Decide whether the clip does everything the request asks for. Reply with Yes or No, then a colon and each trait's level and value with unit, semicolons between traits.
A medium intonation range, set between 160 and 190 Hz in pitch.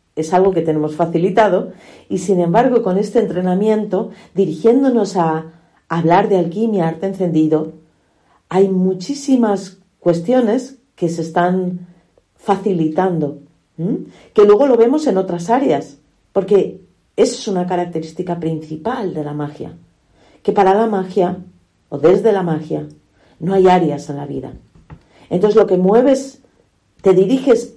Yes: average, 4.7 semitones; medium, 185 Hz